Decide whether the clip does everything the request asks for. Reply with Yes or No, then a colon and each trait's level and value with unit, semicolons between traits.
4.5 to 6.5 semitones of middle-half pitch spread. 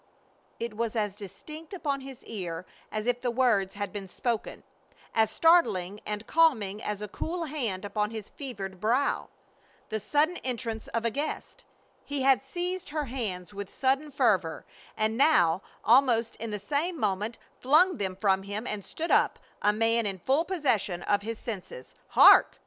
Yes: average, 5.2 semitones